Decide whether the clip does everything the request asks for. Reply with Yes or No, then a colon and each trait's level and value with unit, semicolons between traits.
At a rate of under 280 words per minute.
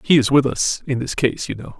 No: fast, 300 wpm